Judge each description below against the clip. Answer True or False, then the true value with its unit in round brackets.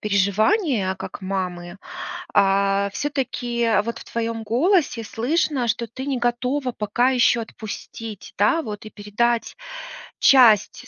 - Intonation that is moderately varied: True (3.7 semitones)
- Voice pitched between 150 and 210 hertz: False (230 Hz)